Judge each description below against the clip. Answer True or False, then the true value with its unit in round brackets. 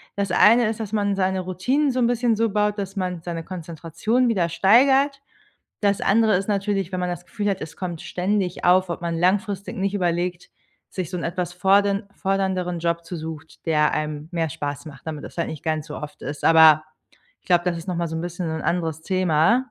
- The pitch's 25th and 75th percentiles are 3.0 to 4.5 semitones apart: True (3.4 semitones)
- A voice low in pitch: False (180 Hz)